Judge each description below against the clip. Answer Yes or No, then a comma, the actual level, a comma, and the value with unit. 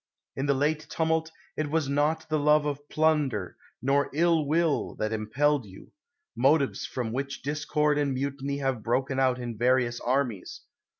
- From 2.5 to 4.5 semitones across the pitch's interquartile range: Yes, average, 2.9 semitones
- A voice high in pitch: No, medium, 140 Hz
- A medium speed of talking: Yes, average, 165 wpm